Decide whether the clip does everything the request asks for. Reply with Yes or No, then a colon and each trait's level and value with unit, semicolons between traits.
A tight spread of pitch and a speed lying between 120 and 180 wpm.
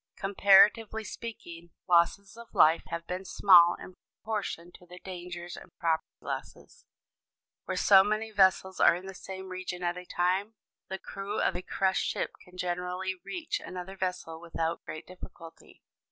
Yes: narrow, 1.9 semitones; average, 155 wpm